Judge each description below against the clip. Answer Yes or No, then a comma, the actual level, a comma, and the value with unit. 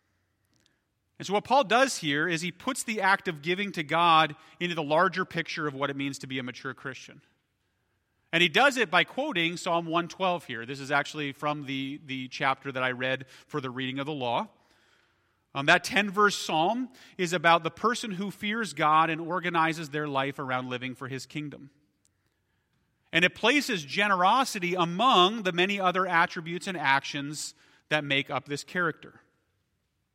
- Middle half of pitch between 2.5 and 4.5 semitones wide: No, average, 5.2 semitones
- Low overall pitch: No, medium, 155 Hz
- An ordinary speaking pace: Yes, average, 180 wpm